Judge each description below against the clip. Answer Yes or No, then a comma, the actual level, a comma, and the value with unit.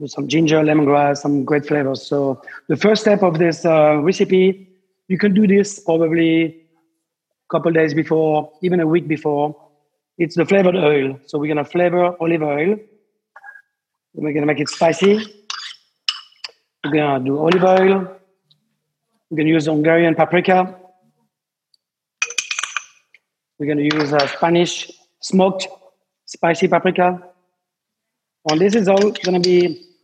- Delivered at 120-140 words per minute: Yes, slow, 135 wpm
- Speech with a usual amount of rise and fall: Yes, average, 3.8 semitones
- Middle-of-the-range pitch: Yes, medium, 170 Hz